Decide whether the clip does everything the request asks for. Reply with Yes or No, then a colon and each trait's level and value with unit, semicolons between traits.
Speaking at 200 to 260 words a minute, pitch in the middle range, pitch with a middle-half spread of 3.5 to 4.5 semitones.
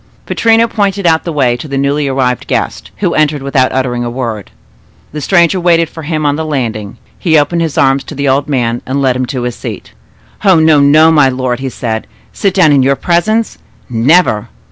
Yes: fast, 205 wpm; medium, 145 Hz; average, 4.1 semitones